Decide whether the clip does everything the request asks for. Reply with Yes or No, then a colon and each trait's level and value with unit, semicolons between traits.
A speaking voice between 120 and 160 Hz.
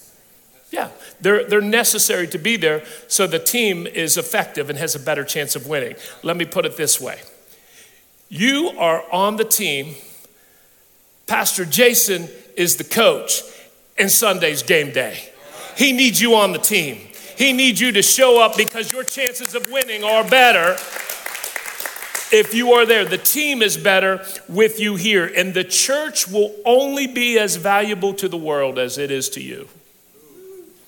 No: high, 215 Hz